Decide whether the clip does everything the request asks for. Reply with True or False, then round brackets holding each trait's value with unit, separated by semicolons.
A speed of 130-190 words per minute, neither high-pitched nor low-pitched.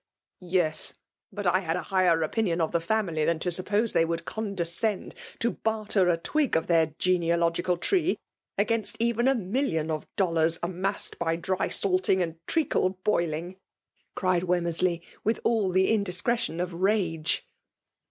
True (155 wpm; 180 Hz)